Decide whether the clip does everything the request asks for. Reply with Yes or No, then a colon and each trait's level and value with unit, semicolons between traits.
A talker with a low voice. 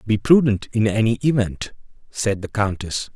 Yes: low, 110 Hz